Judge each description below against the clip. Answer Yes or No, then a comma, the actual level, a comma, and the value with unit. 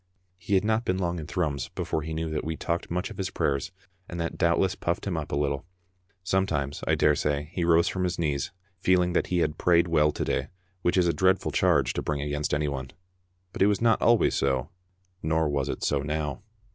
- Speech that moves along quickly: Yes, fast, 220 wpm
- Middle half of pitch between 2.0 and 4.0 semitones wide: Yes, average, 3.6 semitones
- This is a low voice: Yes, very low, 80 Hz